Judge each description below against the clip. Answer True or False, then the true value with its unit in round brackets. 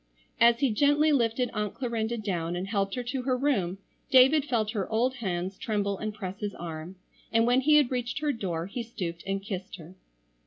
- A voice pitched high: True (220 Hz)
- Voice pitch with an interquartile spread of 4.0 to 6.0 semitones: True (4.6 semitones)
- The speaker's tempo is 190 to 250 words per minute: True (200 wpm)